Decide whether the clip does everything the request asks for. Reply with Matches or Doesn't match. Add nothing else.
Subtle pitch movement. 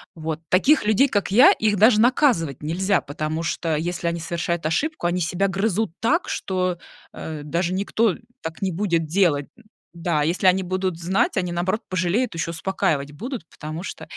Doesn't match